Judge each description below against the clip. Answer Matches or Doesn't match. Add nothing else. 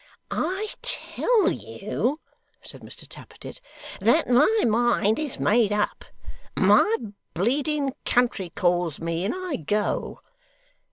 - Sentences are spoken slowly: Matches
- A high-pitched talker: Matches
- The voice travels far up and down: Matches